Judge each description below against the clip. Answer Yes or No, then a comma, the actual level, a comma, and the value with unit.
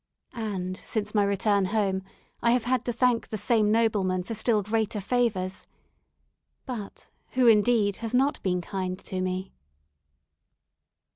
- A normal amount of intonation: Yes, average, 3.4 semitones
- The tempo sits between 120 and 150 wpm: Yes, average, 140 wpm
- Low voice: No, high, 210 Hz